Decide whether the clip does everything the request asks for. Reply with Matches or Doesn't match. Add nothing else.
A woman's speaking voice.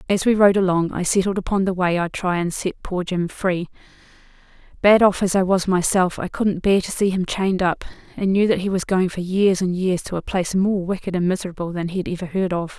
Matches